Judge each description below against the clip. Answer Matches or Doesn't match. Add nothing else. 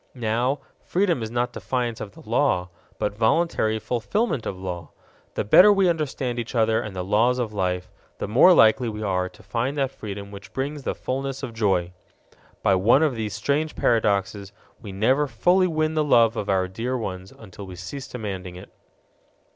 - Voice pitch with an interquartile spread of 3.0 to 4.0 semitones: Doesn't match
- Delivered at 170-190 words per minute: Matches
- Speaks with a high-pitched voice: Doesn't match